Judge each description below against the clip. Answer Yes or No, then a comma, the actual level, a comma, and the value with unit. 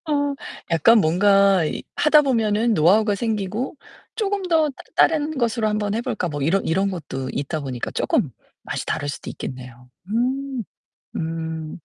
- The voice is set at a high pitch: Yes, high, 205 Hz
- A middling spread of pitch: No, wide, 7.5 semitones